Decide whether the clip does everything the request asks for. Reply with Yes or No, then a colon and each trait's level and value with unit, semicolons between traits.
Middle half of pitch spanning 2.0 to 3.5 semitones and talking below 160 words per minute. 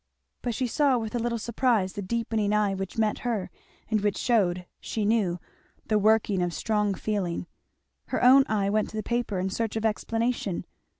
No: average, 2.7 semitones; average, 185 wpm